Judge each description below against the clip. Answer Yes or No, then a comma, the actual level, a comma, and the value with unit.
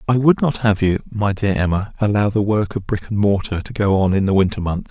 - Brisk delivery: Yes, fast, 270 wpm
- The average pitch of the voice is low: Yes, low, 105 Hz